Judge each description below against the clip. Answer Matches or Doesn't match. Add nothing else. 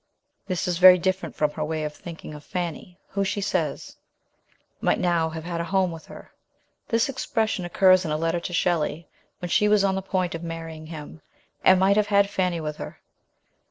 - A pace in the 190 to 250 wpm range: Matches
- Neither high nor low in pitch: Matches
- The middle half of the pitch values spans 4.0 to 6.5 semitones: Doesn't match